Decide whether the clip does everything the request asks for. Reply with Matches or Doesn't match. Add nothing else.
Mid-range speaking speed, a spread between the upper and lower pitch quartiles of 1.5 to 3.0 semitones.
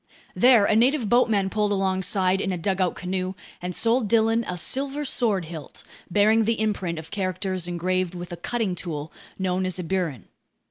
Doesn't match